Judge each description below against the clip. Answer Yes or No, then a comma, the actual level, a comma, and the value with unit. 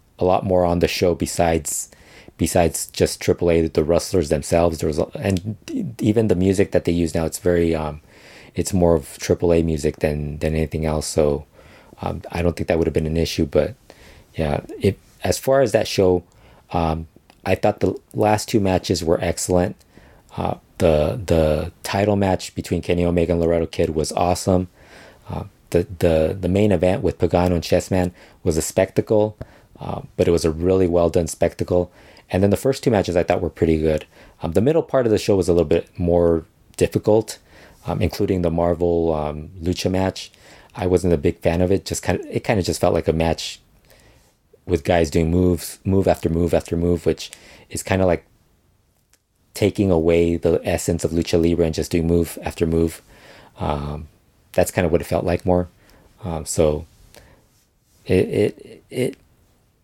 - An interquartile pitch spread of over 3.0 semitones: No, narrow, 2.4 semitones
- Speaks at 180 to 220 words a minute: Yes, average, 190 wpm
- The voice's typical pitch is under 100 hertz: Yes, very low, 85 Hz